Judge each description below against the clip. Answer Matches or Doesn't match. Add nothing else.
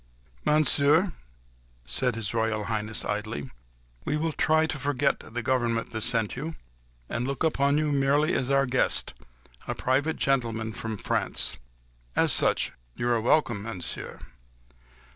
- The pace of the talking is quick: Doesn't match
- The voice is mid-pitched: Doesn't match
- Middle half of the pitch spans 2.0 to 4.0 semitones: Doesn't match